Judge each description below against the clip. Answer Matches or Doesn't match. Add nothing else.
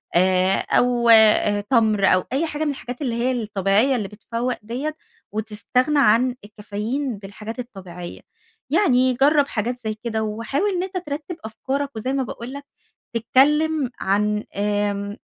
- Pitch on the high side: Matches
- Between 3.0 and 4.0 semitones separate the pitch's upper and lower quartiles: Doesn't match